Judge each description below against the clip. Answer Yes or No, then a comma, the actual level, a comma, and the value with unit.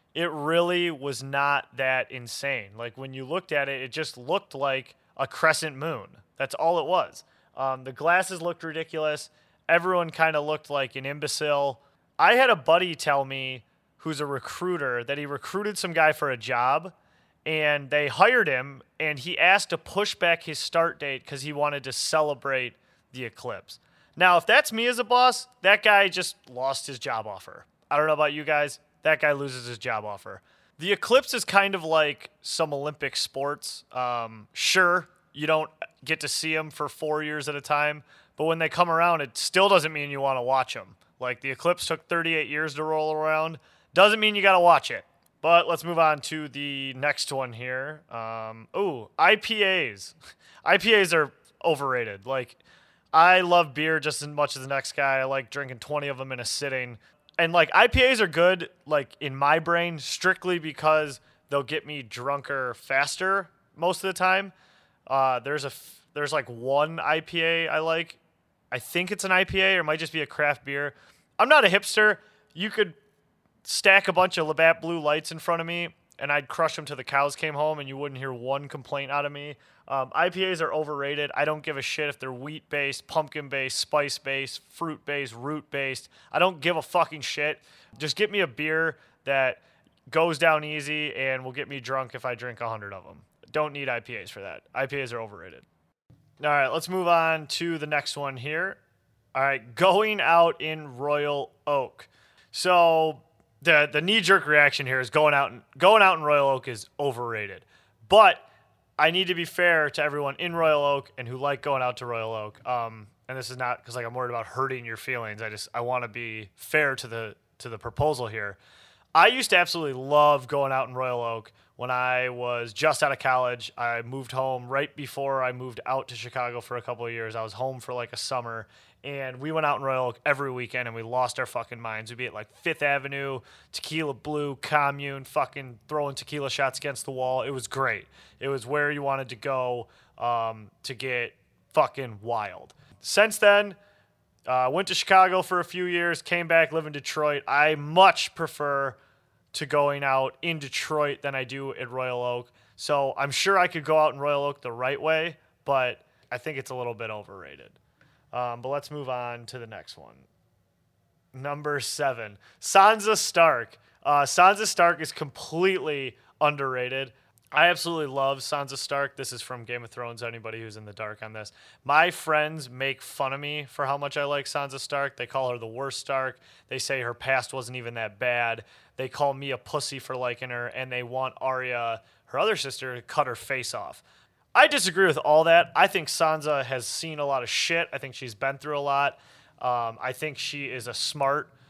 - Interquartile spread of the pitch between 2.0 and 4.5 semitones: Yes, average, 3.7 semitones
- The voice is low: No, medium, 145 Hz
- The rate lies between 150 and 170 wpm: No, fast, 205 wpm